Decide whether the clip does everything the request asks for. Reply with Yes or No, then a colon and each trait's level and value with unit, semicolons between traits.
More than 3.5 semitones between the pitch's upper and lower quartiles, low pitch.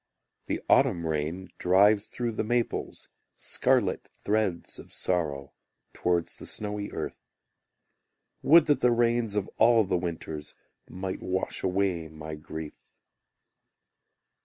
Yes: average, 4.6 semitones; very low, 95 Hz